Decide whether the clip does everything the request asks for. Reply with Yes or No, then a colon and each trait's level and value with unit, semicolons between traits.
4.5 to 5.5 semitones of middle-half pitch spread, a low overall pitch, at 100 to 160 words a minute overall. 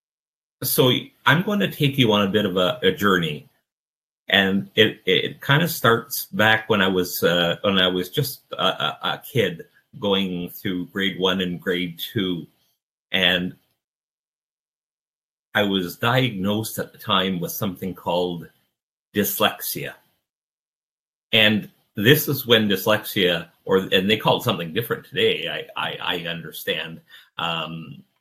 Yes: average, 5.2 semitones; very low, 95 Hz; average, 145 wpm